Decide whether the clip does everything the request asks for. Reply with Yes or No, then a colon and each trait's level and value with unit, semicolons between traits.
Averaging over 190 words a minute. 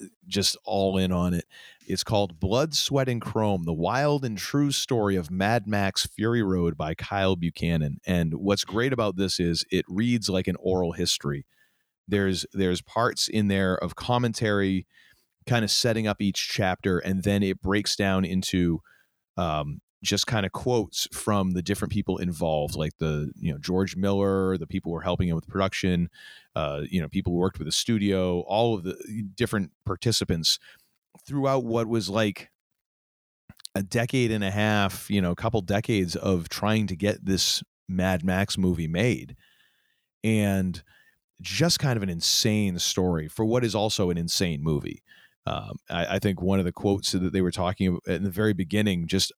No: average, 180 wpm